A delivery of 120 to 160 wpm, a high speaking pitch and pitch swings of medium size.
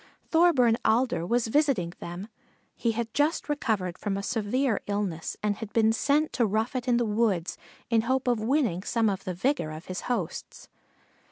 No: average, 180 wpm; high, 225 Hz; average, 4.3 semitones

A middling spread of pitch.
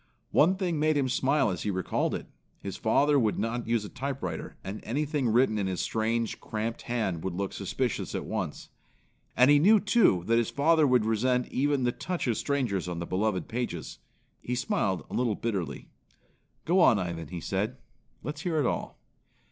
No: wide, 6.1 semitones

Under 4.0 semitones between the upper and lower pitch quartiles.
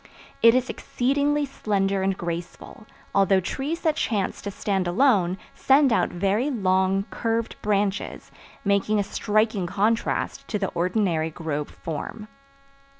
Yes: average, 3.5 semitones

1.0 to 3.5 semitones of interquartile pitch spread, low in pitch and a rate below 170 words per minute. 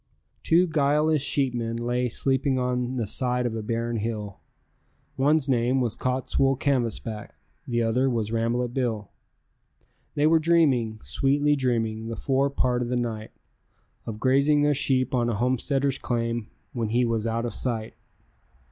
Yes: average, 2.8 semitones; low, 125 Hz; average, 150 wpm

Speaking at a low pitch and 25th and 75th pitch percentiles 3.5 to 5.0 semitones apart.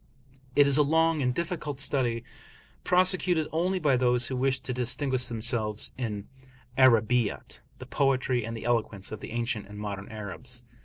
Yes: low, 125 Hz; average, 4.0 semitones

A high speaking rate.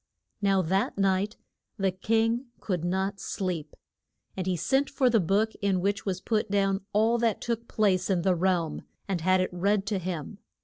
No: average, 180 wpm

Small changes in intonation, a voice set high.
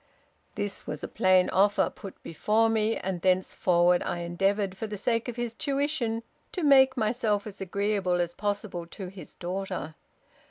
No: average, 3.5 semitones; high, 200 Hz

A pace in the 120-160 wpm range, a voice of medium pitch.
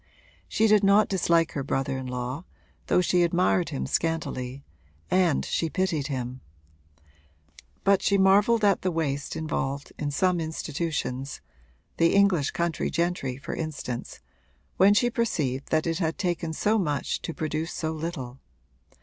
Yes: average, 150 wpm; medium, 165 Hz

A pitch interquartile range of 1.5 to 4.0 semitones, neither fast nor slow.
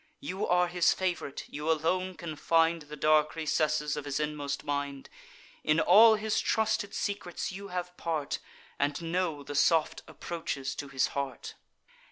Yes: average, 3.6 semitones; average, 155 wpm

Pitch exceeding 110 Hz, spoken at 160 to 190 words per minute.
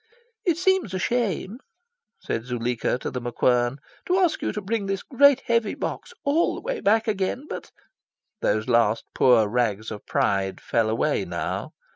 Yes: medium, 185 Hz; average, 170 wpm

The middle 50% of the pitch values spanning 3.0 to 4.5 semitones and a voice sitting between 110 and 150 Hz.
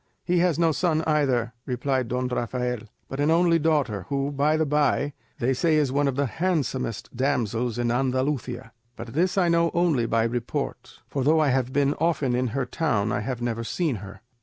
Yes: average, 4.2 semitones; low, 135 Hz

